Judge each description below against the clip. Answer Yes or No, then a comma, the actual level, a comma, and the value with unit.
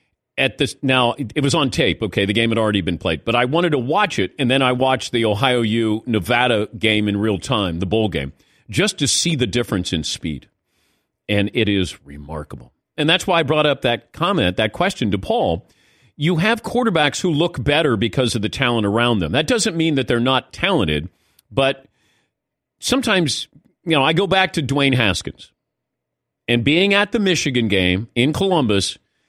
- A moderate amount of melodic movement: No, wide, 6.4 semitones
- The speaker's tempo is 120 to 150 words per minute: No, average, 195 wpm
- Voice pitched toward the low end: Yes, low, 125 Hz